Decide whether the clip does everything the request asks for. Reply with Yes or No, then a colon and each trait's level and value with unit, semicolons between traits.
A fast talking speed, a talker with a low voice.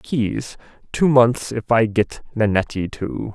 No: average, 145 wpm; low, 115 Hz